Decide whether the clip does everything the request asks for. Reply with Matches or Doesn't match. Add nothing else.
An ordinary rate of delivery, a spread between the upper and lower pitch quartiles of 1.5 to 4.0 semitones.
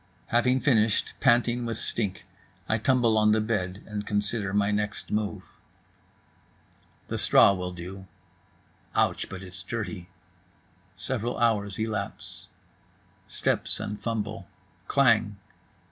Doesn't match